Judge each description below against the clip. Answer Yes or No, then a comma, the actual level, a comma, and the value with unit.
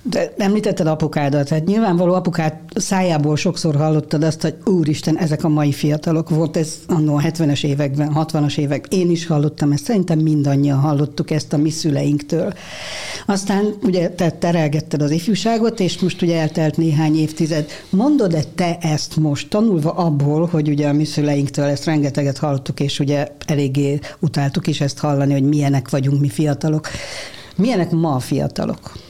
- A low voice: No, medium, 155 Hz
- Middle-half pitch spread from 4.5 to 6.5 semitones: No, narrow, 2.6 semitones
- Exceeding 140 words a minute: Yes, fast, 155 wpm